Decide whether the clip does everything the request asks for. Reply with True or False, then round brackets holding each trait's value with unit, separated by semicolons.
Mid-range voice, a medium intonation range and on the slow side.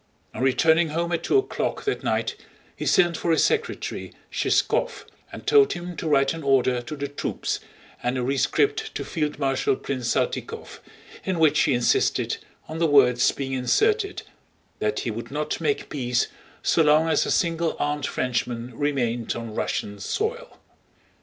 False (145 Hz; 5.0 semitones; 165 wpm)